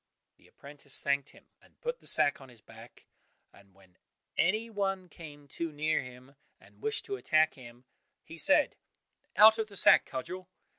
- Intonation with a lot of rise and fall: Yes, wide, 7.1 semitones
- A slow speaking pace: No, average, 180 wpm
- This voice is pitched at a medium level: Yes, medium, 150 Hz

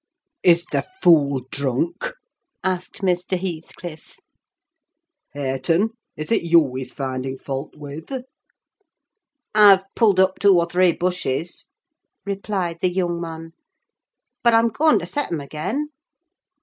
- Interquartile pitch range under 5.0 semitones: Yes, average, 4.2 semitones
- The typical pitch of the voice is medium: Yes, medium, 175 Hz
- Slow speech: Yes, slow, 120 wpm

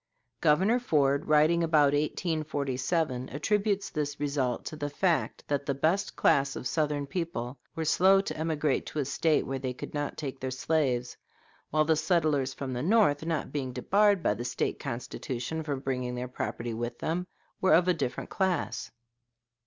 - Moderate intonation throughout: Yes, average, 3.8 semitones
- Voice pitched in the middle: Yes, medium, 150 Hz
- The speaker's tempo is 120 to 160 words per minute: No, average, 170 wpm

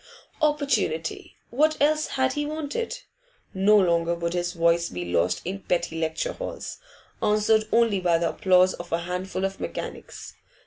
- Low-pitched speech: No, high, 190 Hz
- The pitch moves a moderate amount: No, wide, 7.5 semitones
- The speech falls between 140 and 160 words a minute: Yes, average, 150 wpm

